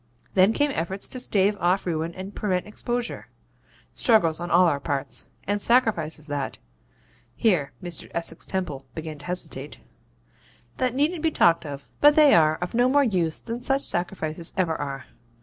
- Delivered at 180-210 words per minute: No, average, 165 wpm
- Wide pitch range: Yes, wide, 6.4 semitones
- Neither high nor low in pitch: Yes, medium, 180 Hz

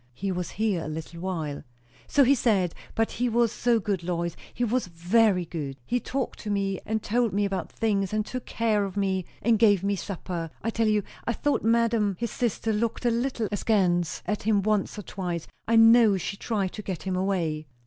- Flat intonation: No, average, 3.8 semitones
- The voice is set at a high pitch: Yes, high, 205 Hz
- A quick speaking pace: Yes, fast, 210 wpm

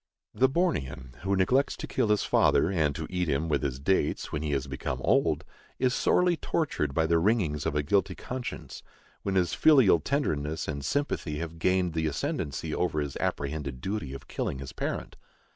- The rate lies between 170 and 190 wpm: Yes, average, 185 wpm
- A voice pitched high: No, very low, 80 Hz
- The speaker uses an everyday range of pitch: No, wide, 5.7 semitones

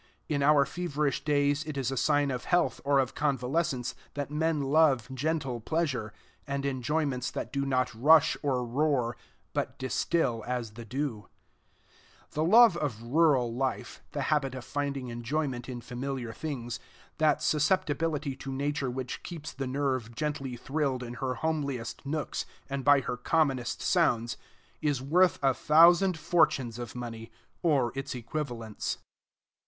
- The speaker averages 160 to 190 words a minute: No, average, 150 wpm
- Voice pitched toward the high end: No, low, 135 Hz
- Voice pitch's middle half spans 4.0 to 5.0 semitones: No, average, 3.4 semitones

